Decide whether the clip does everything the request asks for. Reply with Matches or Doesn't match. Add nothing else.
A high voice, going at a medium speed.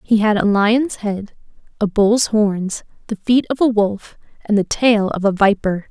Matches